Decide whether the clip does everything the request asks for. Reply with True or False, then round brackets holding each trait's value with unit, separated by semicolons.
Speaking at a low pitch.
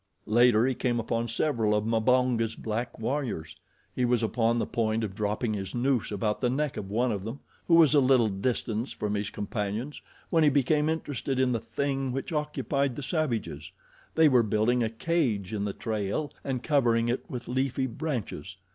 True (120 Hz)